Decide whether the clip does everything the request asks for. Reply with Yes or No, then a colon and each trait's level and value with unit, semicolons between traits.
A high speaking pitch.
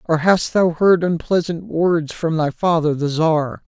No: medium, 165 Hz